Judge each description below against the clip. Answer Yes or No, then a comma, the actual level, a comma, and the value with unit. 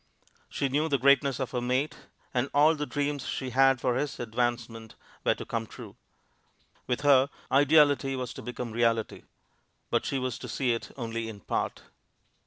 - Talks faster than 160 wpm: Yes, average, 175 wpm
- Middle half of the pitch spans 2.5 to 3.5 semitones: Yes, average, 2.8 semitones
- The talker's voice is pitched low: Yes, low, 130 Hz